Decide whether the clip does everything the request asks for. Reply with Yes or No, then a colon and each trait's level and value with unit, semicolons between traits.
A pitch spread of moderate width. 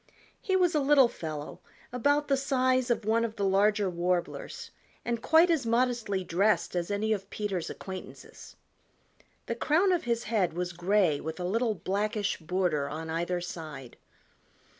No: wide, 5.8 semitones